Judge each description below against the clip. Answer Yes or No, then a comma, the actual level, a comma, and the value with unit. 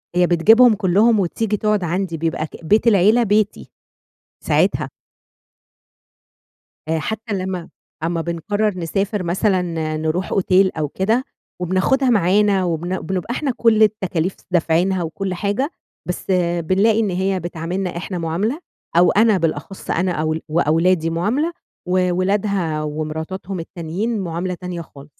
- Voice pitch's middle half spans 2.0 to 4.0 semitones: Yes, average, 3.6 semitones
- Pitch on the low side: No, medium, 185 Hz